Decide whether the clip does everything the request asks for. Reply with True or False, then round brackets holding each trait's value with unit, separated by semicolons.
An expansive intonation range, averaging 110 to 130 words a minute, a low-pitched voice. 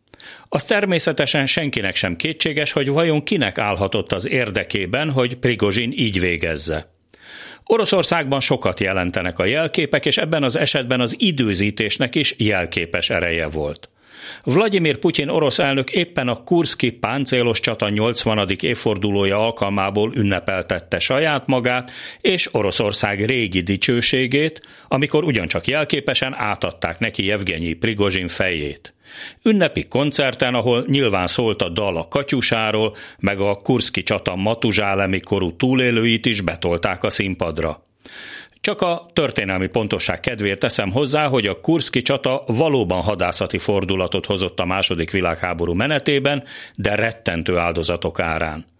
True (6.1 semitones; 125 wpm; 115 Hz)